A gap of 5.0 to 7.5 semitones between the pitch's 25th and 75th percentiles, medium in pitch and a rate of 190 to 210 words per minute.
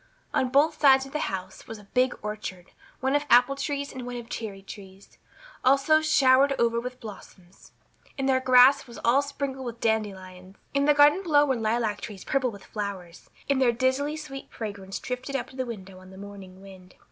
No: average, 5.3 semitones; high, 245 Hz; average, 195 wpm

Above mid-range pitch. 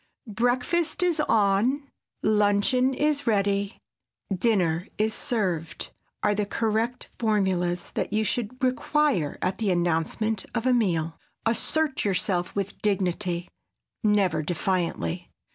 Yes: high, 210 Hz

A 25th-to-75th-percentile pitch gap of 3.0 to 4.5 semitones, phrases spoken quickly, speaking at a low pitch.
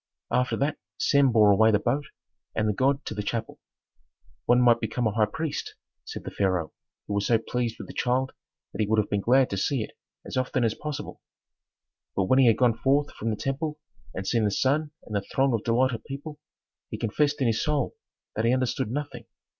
Yes: average, 3.9 semitones; fast, 215 wpm; low, 120 Hz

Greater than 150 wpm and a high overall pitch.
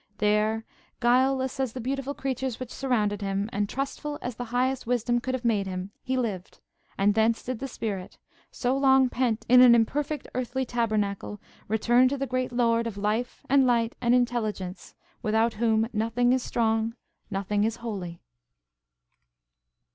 Yes: average, 160 wpm; high, 235 Hz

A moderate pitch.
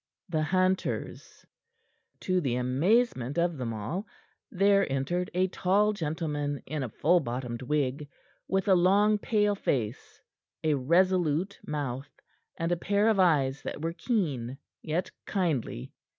Yes: medium, 165 Hz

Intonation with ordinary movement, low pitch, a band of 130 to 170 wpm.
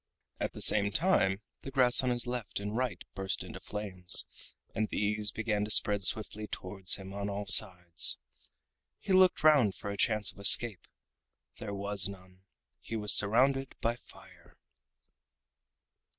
Yes: average, 3.2 semitones; low, 105 Hz; average, 150 wpm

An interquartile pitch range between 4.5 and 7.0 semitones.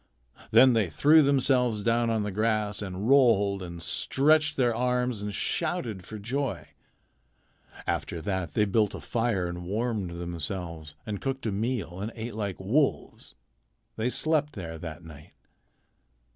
Yes: average, 5.1 semitones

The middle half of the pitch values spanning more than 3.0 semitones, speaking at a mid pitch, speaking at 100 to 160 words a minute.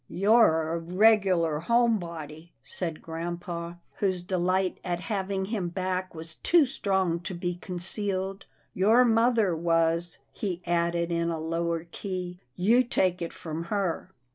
No: narrow, 2.6 semitones; medium, 180 Hz; average, 150 wpm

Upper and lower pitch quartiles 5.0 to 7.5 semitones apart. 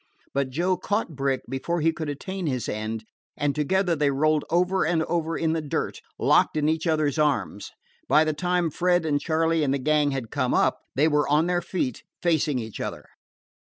No: average, 3.3 semitones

